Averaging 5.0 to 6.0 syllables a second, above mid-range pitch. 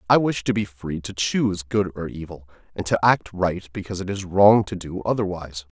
No: 5.5 syllables/s; very low, 95 Hz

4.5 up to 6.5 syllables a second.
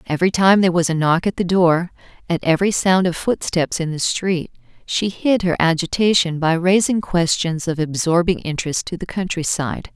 Yes: 5.3 syllables/s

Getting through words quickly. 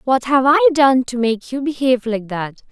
Yes: fast, 220 wpm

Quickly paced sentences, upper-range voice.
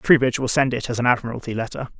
No: fast, 240 wpm; low, 120 Hz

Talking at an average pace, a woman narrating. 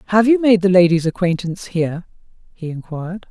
Yes: average, 165 wpm; female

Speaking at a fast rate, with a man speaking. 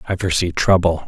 No: average, 165 wpm; male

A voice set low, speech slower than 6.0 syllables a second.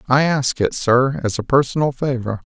Yes: low, 130 Hz; 4.9 syllables/s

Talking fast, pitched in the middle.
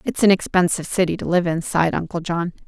Yes: fast, 225 wpm; medium, 175 Hz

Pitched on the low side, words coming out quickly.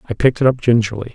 Yes: low, 120 Hz; fast, 265 wpm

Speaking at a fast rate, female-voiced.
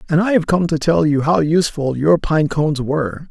No: fast, 235 wpm; male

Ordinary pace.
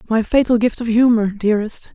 Yes: average, 185 wpm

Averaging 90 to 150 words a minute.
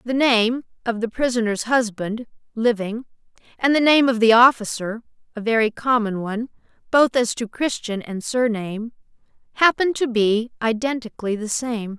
Yes: average, 145 wpm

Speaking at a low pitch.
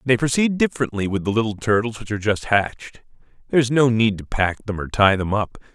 Yes: low, 115 Hz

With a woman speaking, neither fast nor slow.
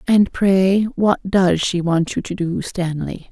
Yes: female; average, 180 wpm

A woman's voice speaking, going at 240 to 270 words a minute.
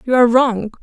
No: female; fast, 215 wpm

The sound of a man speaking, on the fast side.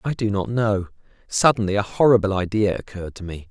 No: male; average, 190 wpm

